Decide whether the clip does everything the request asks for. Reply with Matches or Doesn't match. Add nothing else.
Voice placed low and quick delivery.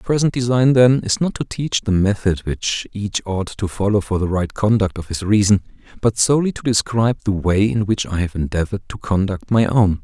Matches